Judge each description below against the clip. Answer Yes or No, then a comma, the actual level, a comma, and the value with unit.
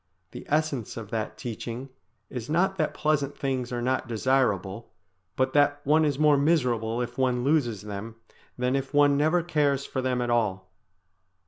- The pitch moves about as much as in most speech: Yes, average, 3.8 semitones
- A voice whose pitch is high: No, low, 130 Hz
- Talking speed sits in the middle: Yes, average, 165 wpm